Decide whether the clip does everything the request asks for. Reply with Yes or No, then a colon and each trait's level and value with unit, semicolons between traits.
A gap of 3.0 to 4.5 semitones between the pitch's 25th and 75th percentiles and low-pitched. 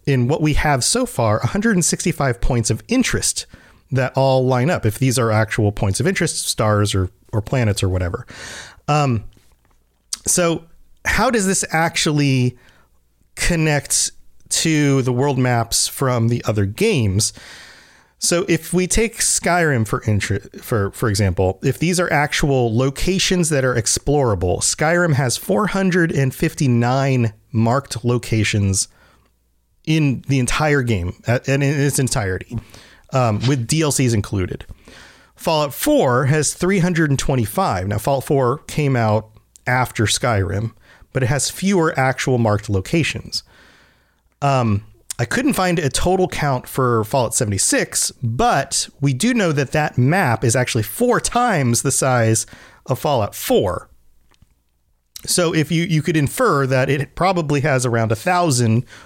No: wide, 5.6 semitones; low, 130 Hz